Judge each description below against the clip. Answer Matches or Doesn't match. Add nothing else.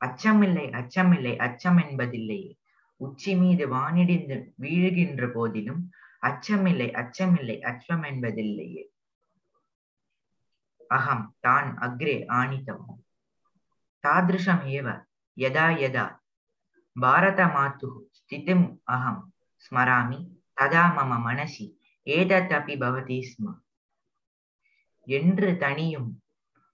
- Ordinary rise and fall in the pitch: Doesn't match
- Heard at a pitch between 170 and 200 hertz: Doesn't match